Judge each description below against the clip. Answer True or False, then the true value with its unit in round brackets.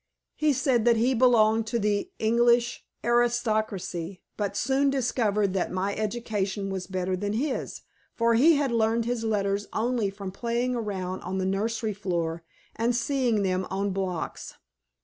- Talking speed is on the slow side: False (150 wpm)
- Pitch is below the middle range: False (220 Hz)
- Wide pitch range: False (3.5 semitones)